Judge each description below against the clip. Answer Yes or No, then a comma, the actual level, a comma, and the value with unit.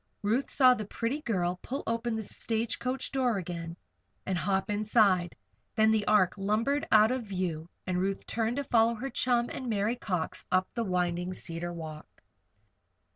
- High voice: Yes, high, 215 Hz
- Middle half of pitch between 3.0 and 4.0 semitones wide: No, average, 4.5 semitones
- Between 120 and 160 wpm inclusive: No, average, 170 wpm